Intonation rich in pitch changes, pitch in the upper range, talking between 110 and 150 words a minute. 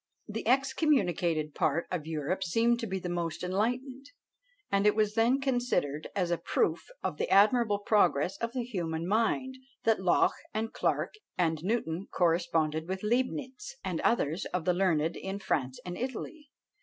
No: wide, 5.9 semitones; high, 195 Hz; average, 160 wpm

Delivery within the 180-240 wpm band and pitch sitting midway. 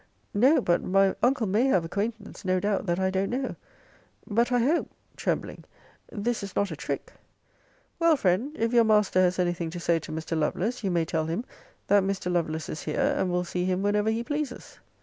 No: average, 200 wpm; high, 200 Hz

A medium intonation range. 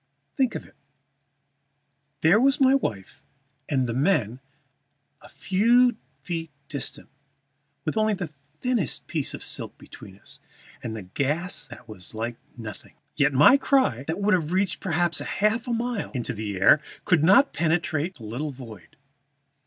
No: wide, 9.0 semitones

